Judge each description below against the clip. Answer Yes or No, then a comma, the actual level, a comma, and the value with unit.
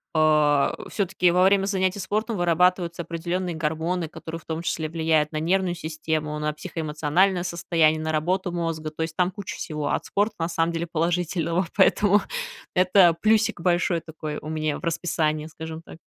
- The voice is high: No, medium, 170 Hz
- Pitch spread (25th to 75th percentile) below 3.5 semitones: Yes, narrow, 2.5 semitones